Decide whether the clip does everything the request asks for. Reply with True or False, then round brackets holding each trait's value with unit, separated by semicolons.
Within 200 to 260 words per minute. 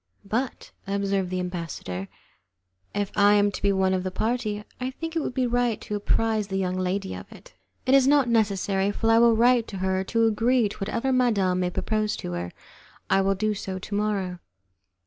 True (205 wpm)